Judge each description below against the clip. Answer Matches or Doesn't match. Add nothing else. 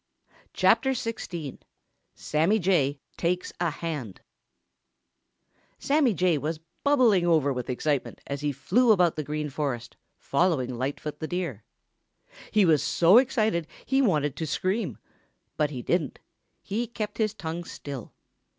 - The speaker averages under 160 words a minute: Matches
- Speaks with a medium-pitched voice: Matches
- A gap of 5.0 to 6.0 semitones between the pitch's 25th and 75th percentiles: Matches